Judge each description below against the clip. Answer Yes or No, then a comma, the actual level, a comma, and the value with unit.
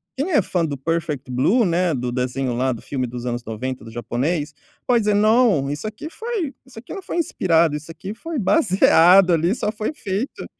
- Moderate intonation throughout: No, wide, 8.8 semitones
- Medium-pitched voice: Yes, medium, 170 Hz